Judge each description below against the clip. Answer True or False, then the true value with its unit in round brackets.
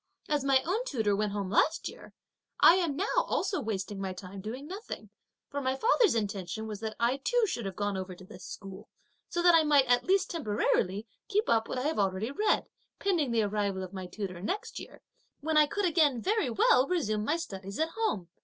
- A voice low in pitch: False (240 Hz)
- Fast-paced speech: True (210 wpm)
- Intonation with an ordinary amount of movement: False (8.6 semitones)